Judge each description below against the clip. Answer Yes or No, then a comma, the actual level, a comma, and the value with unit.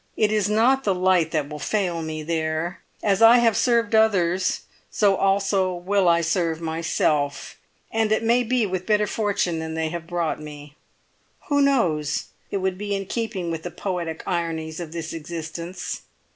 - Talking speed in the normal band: Yes, average, 175 wpm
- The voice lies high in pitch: No, medium, 180 Hz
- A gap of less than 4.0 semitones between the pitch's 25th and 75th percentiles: No, average, 4.3 semitones